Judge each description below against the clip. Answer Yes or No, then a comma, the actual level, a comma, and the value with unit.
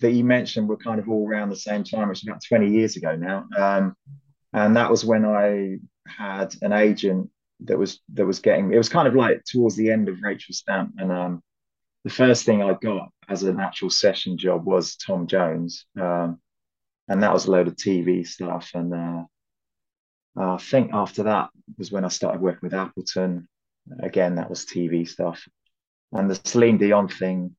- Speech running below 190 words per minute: No, average, 195 wpm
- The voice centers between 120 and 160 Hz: No, very low, 95 Hz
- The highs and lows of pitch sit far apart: No, average, 3.3 semitones